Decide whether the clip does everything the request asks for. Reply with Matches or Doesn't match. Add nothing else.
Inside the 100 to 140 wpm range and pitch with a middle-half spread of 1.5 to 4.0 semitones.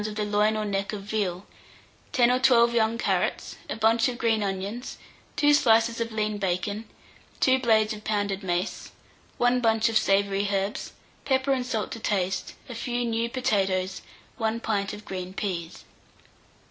Doesn't match